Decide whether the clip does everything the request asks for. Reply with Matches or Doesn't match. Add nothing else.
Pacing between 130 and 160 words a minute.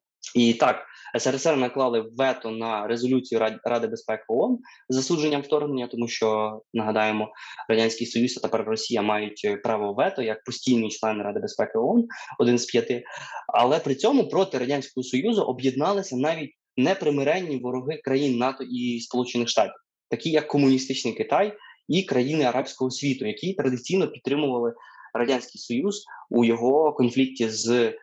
Matches